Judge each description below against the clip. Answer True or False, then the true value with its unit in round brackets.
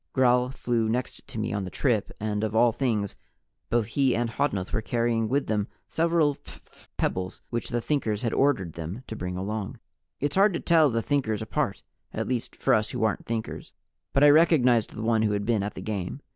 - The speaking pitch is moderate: False (115 Hz)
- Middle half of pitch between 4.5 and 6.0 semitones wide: False (3.8 semitones)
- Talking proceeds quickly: True (210 wpm)